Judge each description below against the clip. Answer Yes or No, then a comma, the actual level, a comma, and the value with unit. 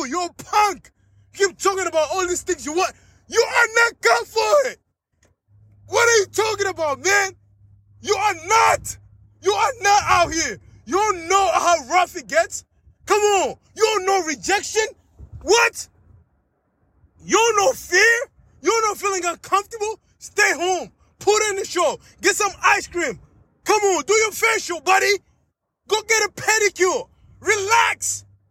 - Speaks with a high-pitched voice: Yes, very high, 390 Hz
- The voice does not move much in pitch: No, average, 4.0 semitones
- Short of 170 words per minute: Yes, average, 160 wpm